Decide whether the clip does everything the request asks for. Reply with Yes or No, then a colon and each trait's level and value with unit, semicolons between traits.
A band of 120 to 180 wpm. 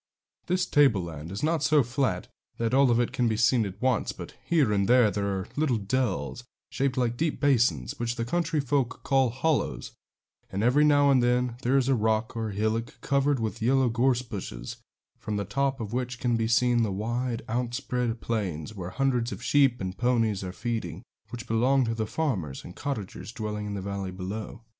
No: average, 195 wpm